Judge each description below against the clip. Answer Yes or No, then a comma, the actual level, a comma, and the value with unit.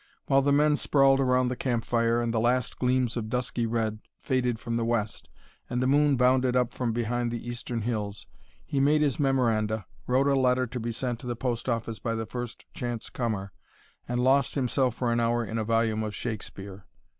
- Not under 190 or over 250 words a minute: Yes, average, 200 wpm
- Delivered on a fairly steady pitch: Yes, narrow, 2.0 semitones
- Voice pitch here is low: Yes, low, 120 Hz